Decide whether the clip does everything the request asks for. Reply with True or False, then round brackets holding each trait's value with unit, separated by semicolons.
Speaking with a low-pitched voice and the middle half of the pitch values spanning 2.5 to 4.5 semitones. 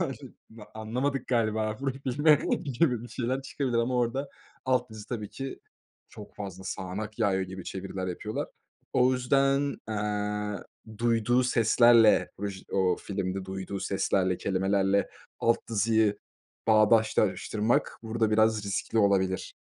True (110 Hz; 3.5 semitones)